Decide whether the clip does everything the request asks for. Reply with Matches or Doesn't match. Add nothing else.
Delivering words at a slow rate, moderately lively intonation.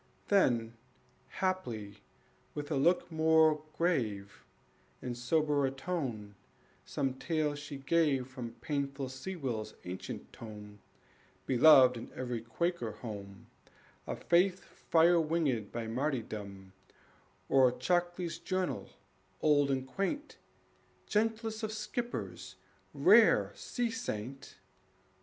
Doesn't match